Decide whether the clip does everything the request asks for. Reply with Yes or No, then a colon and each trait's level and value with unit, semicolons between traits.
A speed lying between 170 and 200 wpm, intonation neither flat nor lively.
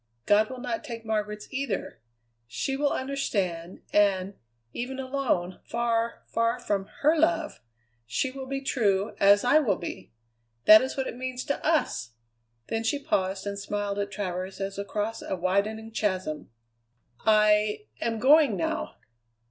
No: average, 150 wpm; average, 4.7 semitones